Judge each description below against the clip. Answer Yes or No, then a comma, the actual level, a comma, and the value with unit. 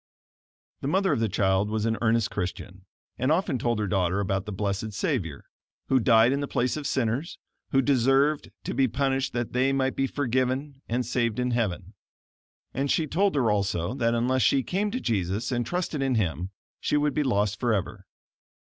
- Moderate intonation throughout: Yes, average, 4.6 semitones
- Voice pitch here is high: No, low, 120 Hz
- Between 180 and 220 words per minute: Yes, average, 190 wpm